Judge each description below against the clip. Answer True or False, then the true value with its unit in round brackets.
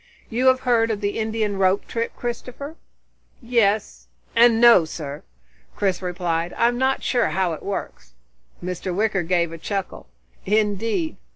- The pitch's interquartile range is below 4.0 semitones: False (4.4 semitones)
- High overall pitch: True (210 Hz)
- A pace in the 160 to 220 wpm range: False (145 wpm)